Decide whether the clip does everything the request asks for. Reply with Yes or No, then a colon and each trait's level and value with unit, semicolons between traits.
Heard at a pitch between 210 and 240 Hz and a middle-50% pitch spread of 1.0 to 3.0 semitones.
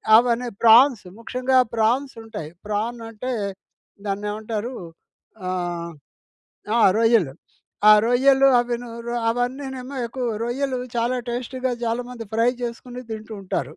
Yes: high, 235 Hz; narrow, 2.5 semitones